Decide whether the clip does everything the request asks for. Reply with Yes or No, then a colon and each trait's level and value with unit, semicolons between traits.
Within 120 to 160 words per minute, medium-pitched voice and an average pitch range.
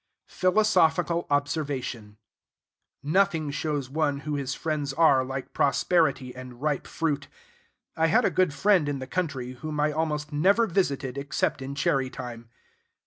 Yes: average, 140 wpm; medium, 145 Hz; average, 3.2 semitones